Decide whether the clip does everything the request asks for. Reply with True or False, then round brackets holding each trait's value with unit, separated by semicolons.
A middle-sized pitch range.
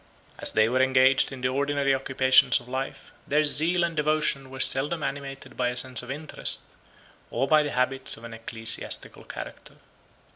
False (2.2 semitones)